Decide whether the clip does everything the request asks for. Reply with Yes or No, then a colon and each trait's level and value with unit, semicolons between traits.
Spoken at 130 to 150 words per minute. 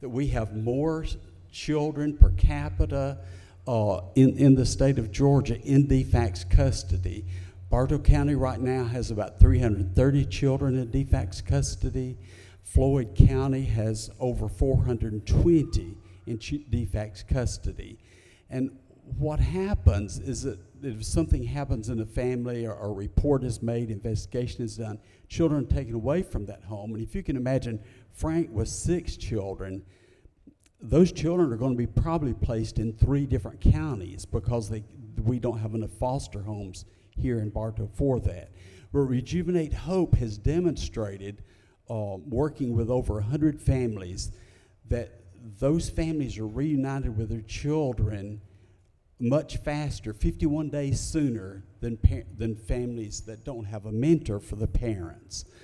Yes: average, 145 wpm